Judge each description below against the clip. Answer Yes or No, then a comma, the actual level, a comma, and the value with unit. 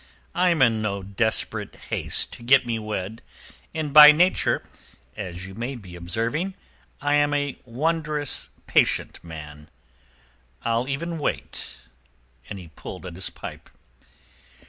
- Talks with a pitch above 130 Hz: No, low, 115 Hz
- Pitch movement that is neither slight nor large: No, wide, 7.4 semitones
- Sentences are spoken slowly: Yes, slow, 125 wpm